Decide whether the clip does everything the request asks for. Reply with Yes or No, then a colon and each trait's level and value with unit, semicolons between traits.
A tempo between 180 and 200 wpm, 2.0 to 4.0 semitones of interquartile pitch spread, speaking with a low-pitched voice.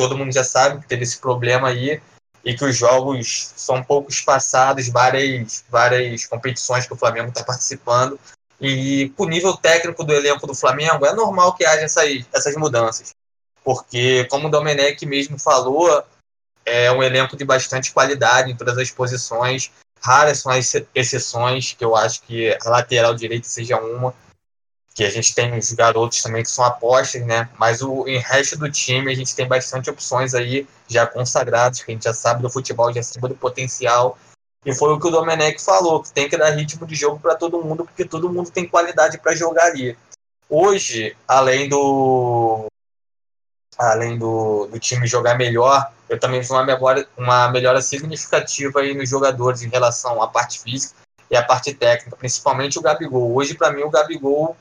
Yes: fast, 185 wpm; average, 2.8 semitones; low, 130 Hz